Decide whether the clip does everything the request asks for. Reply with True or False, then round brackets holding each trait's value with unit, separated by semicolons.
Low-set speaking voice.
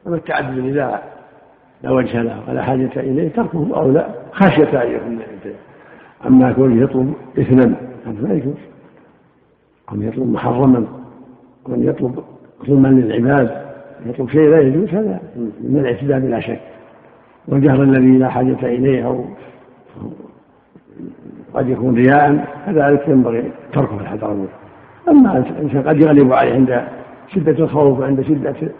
True (130 Hz)